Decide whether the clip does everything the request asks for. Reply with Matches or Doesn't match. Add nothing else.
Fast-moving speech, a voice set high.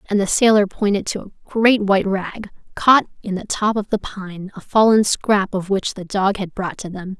Matches